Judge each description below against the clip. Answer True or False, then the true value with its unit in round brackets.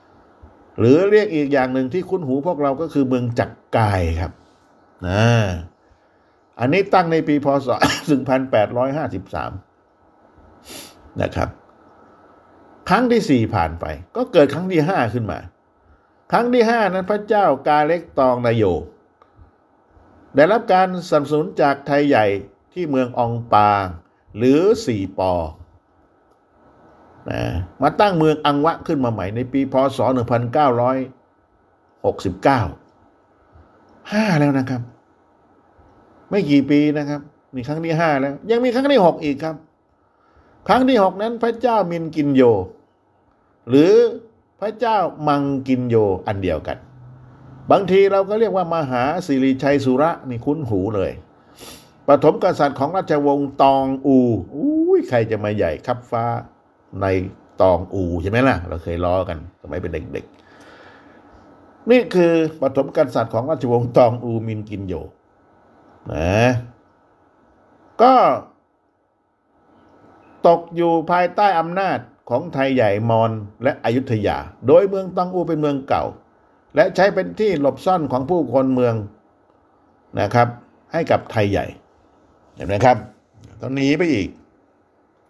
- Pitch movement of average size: False (6.5 semitones)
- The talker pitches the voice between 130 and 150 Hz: True (135 Hz)